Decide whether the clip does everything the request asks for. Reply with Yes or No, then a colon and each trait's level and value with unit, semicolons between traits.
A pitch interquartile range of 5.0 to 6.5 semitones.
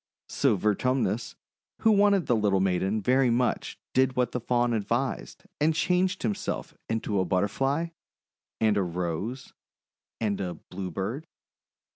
Yes: average, 5.3 semitones